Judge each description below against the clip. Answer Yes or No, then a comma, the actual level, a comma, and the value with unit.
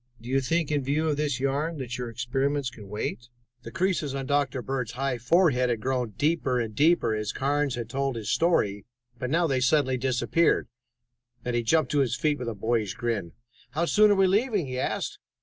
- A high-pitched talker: No, low, 130 Hz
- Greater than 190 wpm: Yes, fast, 205 wpm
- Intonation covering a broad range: No, average, 4.0 semitones